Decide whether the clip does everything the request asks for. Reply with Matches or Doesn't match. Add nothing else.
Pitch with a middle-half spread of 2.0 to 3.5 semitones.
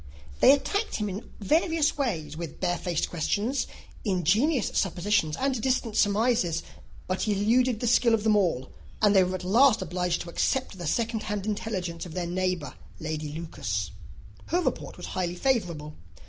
Doesn't match